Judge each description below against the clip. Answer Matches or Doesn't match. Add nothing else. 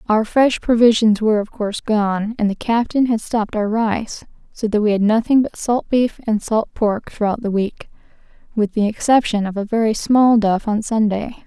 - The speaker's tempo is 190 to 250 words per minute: Matches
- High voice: Matches